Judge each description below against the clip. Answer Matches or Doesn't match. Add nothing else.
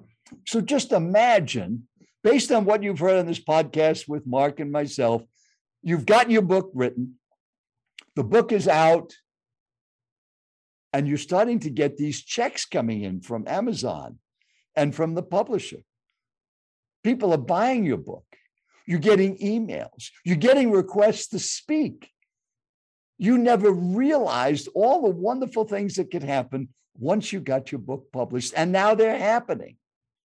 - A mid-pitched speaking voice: Matches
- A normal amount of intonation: Doesn't match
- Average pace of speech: Matches